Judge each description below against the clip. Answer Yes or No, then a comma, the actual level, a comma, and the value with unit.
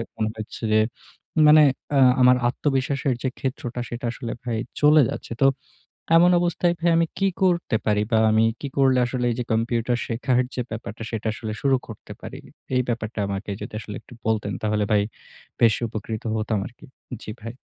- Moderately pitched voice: No, low, 120 Hz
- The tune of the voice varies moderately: Yes, average, 3.6 semitones